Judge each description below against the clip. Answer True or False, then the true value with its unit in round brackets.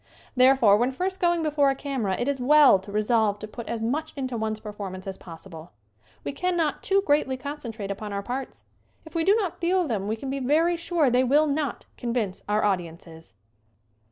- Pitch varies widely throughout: True (6.3 semitones)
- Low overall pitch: False (255 Hz)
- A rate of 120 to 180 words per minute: False (195 wpm)